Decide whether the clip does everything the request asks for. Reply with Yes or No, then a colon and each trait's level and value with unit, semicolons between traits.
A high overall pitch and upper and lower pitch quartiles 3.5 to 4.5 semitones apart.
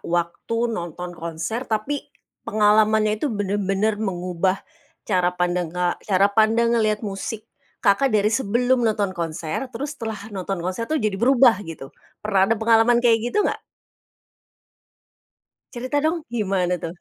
Yes: high, 210 Hz; average, 3.9 semitones